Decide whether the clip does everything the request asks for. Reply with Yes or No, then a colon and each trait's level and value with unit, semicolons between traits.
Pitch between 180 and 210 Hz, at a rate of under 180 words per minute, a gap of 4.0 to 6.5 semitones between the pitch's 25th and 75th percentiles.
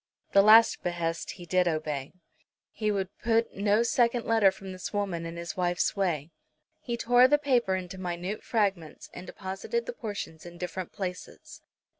Yes: high, 190 Hz; average, 165 wpm; average, 4.3 semitones